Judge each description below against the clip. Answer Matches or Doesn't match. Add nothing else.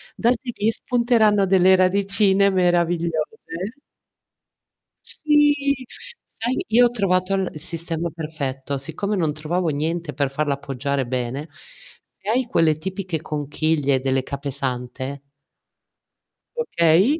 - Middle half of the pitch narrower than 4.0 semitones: Doesn't match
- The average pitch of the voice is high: Doesn't match